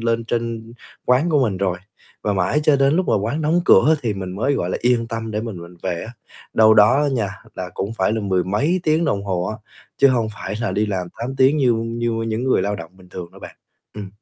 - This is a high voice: No, low, 115 Hz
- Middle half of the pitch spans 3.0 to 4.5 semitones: No, average, 5.0 semitones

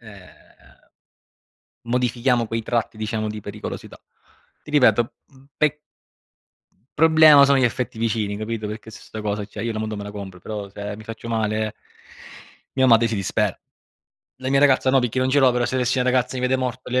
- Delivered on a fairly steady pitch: No, average, 3.1 semitones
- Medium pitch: No, low, 115 Hz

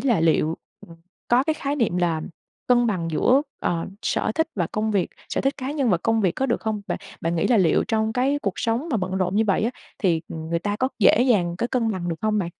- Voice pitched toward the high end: Yes, high, 215 Hz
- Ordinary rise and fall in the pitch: No, wide, 5.8 semitones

